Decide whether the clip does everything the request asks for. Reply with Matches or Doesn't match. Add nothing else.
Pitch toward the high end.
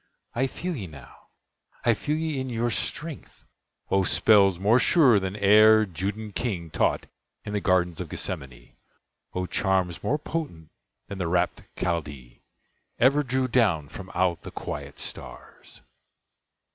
Doesn't match